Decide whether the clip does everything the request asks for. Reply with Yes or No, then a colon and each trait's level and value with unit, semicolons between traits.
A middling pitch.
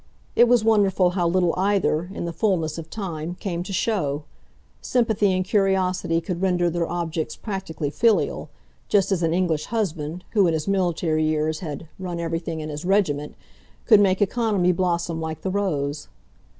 Yes: medium, 175 Hz